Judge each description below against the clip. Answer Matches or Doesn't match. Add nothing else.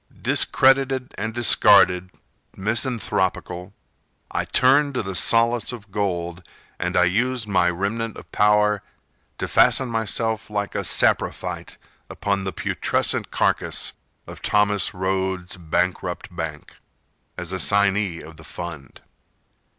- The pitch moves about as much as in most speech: Matches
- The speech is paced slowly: Matches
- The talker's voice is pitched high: Doesn't match